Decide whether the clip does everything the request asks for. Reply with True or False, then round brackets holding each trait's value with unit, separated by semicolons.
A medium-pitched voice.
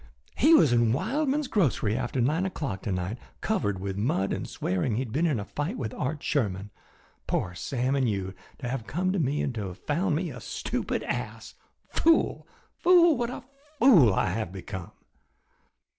False (130 Hz)